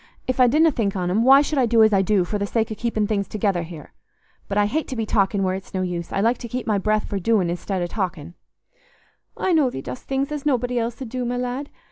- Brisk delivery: Yes, fast, 270 wpm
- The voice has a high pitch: Yes, high, 220 Hz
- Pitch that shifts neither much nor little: Yes, average, 4.4 semitones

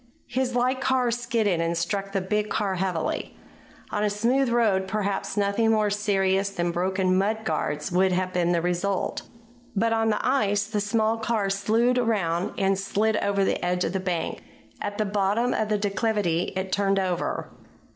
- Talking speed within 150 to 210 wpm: Yes, average, 175 wpm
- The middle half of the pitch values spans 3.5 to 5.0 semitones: No, average, 2.7 semitones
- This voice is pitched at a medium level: No, high, 200 Hz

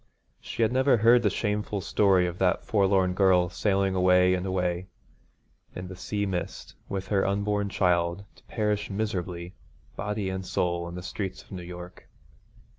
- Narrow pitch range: Yes, narrow, 2.3 semitones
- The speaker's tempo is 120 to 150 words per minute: No, average, 165 wpm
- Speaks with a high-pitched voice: No, very low, 95 Hz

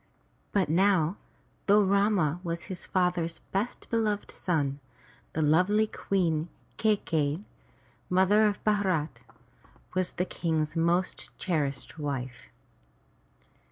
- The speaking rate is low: Yes, slow, 105 wpm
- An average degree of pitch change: Yes, average, 4.2 semitones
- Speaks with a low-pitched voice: No, medium, 180 Hz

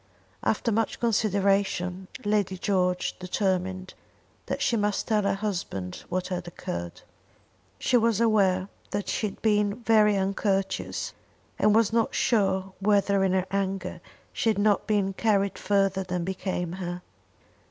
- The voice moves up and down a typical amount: No, narrow, 2.1 semitones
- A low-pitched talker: No, high, 195 Hz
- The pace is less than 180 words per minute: Yes, average, 140 wpm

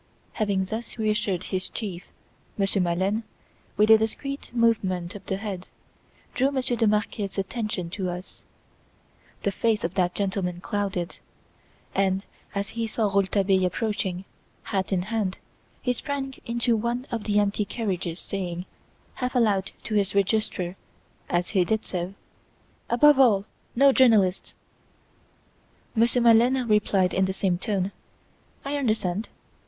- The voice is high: Yes, high, 205 Hz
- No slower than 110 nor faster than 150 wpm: Yes, slow, 135 wpm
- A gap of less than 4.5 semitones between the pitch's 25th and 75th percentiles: Yes, average, 3.3 semitones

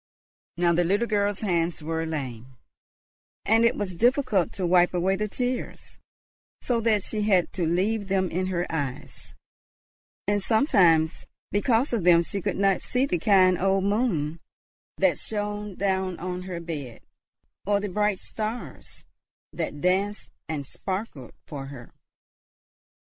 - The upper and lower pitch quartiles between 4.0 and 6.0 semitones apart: No, average, 3.6 semitones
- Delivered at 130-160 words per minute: Yes, average, 140 wpm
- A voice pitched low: No, high, 190 Hz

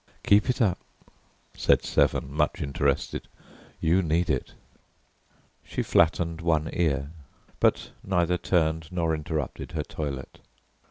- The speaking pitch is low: Yes, very low, 80 Hz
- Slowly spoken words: Yes, slow, 115 wpm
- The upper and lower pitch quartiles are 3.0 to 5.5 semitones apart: No, narrow, 2.5 semitones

